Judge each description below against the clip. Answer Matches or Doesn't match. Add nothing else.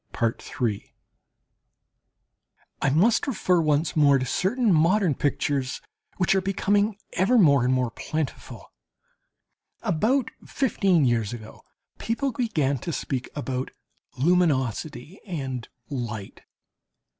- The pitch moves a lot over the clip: Matches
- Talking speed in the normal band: Doesn't match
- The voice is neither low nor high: Matches